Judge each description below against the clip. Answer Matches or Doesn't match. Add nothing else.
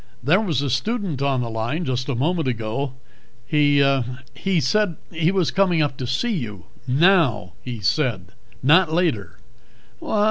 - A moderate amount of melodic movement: Doesn't match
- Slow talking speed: Doesn't match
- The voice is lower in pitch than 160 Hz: Matches